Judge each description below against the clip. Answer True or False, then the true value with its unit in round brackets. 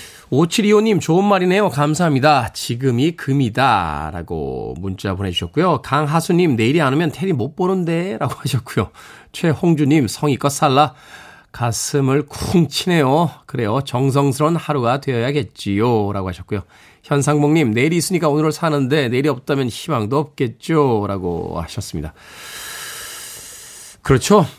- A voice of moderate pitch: True (145 Hz)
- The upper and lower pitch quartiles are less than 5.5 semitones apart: True (5.1 semitones)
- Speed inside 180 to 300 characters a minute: False (310 characters per minute)